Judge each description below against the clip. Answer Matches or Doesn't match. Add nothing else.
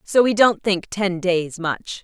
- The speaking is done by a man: Doesn't match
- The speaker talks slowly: Doesn't match